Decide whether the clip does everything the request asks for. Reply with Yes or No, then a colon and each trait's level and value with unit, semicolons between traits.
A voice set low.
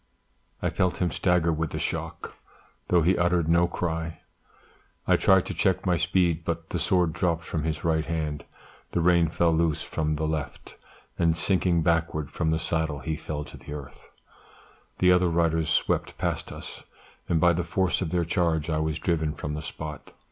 Yes: very low, 80 Hz